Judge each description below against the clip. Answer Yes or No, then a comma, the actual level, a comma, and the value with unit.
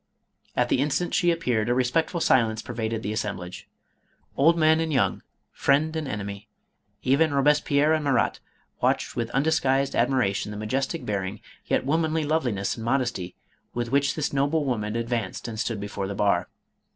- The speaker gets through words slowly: No, average, 170 wpm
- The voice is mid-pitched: No, low, 130 Hz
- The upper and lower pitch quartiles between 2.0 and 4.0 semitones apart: No, wide, 5.5 semitones